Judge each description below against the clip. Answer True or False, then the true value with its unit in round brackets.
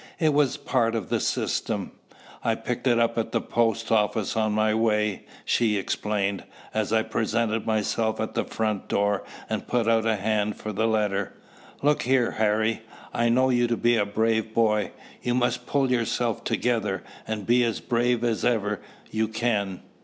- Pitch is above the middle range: False (110 Hz)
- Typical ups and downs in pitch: False (1.8 semitones)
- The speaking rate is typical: True (180 wpm)